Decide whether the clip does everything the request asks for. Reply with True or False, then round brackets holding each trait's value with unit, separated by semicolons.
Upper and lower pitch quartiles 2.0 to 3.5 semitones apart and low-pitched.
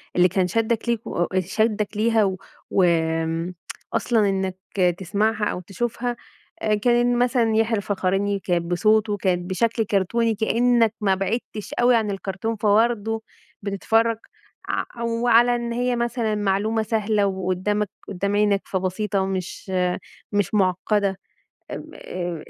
False (3.1 semitones; 210 Hz)